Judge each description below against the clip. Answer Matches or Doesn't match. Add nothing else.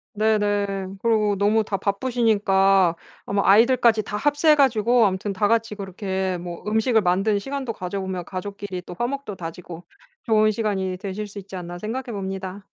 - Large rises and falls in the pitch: Doesn't match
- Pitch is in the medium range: Doesn't match